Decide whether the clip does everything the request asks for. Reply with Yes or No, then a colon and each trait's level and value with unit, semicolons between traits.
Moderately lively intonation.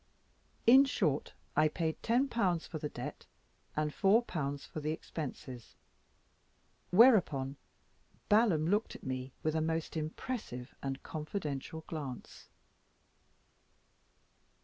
No: wide, 5.9 semitones